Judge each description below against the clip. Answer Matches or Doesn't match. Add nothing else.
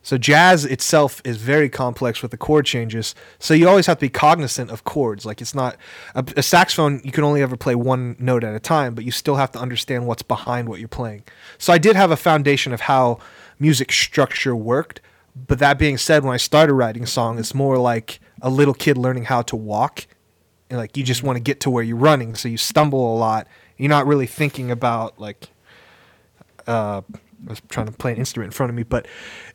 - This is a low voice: Matches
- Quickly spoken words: Matches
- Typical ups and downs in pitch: Matches